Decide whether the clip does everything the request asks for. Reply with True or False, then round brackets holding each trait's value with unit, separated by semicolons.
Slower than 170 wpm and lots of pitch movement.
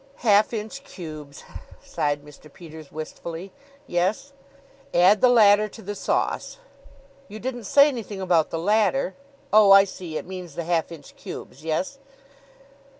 False (150 wpm; 4.8 semitones)